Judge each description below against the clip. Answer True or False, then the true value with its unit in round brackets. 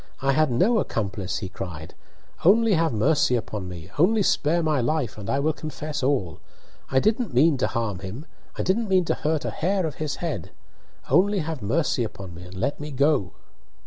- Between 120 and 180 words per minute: False (195 wpm)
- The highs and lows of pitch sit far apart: True (7.8 semitones)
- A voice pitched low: False (145 Hz)